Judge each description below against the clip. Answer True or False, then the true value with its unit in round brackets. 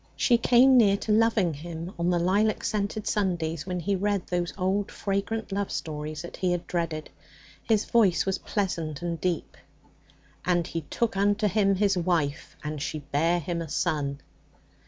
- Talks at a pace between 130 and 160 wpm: False (170 wpm)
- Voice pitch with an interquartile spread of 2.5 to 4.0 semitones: True (3.6 semitones)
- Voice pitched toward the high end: False (180 Hz)